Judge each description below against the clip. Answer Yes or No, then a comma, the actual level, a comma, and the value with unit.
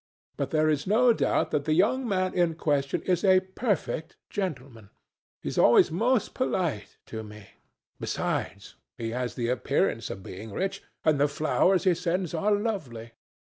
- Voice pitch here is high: No, medium, 160 Hz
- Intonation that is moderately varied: No, wide, 7.1 semitones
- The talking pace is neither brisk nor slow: Yes, average, 165 wpm